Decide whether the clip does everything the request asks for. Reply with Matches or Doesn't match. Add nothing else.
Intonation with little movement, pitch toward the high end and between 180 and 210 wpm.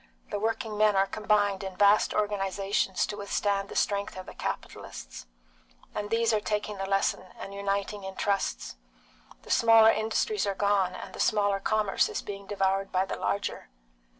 Doesn't match